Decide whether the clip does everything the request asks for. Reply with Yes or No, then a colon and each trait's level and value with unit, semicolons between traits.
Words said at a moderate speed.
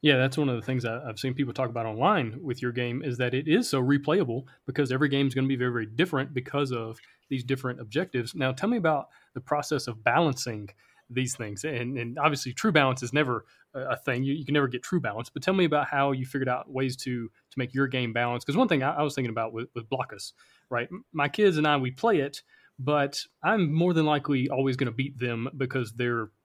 No: fast, 245 wpm